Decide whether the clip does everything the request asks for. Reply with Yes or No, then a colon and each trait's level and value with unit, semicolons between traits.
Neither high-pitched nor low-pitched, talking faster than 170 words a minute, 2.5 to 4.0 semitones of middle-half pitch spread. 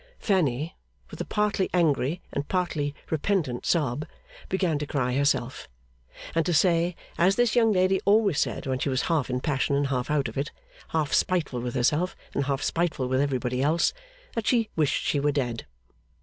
No: medium, 150 Hz; average, 180 wpm; average, 5.1 semitones